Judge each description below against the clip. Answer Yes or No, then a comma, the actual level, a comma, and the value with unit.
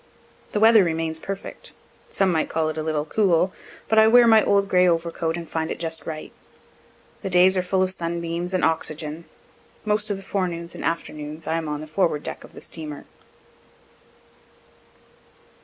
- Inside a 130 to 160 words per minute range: No, average, 175 wpm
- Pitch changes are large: No, average, 3.1 semitones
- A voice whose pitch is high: No, medium, 170 Hz